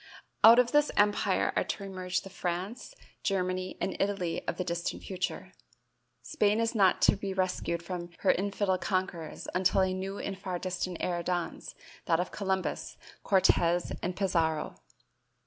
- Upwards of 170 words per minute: No, average, 155 wpm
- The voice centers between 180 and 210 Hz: Yes, medium, 185 Hz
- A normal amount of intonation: No, narrow, 1.8 semitones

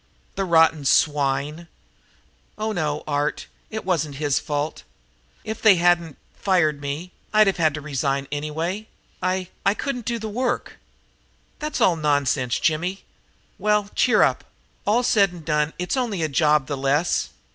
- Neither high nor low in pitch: Yes, medium, 165 Hz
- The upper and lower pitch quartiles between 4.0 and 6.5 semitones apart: Yes, average, 5.2 semitones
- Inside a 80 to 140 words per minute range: No, average, 150 wpm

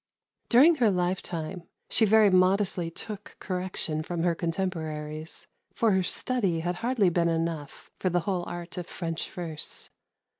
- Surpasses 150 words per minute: No, average, 145 wpm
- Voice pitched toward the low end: No, medium, 180 Hz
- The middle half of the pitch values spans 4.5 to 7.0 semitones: No, average, 2.8 semitones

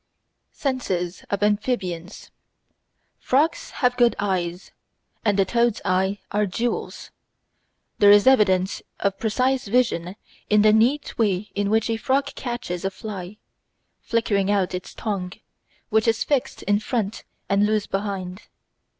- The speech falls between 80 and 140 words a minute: Yes, slow, 135 wpm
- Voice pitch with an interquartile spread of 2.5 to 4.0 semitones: Yes, average, 3.5 semitones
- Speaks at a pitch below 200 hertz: No, high, 210 Hz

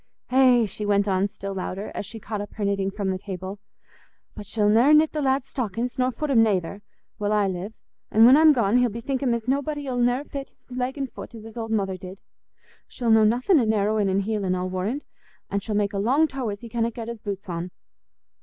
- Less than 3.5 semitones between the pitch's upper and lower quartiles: No, average, 3.9 semitones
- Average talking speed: No, fast, 230 wpm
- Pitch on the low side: No, high, 220 Hz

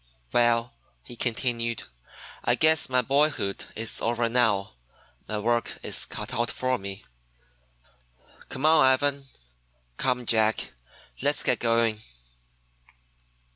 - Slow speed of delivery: Yes, slow, 110 wpm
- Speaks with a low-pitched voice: Yes, low, 120 Hz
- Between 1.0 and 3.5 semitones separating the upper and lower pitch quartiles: Yes, narrow, 2.6 semitones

